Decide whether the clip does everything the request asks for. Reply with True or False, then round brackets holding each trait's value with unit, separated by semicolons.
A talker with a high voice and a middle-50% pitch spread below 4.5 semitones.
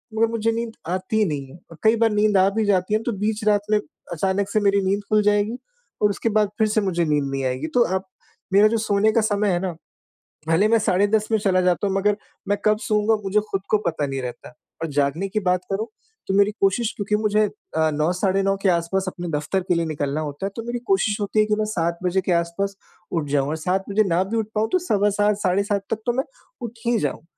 True (200 Hz; 3.2 semitones)